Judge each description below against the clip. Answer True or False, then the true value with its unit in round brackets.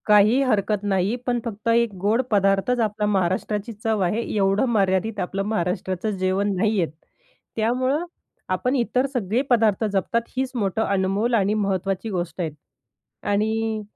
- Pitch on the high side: True (210 Hz)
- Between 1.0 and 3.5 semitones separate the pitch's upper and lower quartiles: True (2.7 semitones)